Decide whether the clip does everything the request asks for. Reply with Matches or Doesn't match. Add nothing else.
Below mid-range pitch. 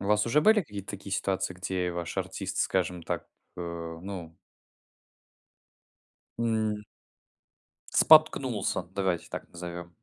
Matches